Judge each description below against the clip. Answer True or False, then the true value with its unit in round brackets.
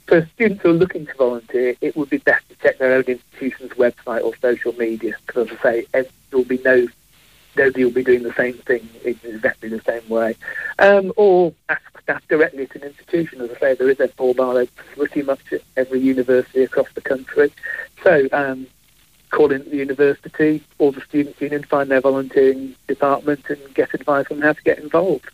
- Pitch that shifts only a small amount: False (3.1 semitones)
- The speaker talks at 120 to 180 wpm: False (195 wpm)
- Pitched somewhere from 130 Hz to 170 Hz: True (135 Hz)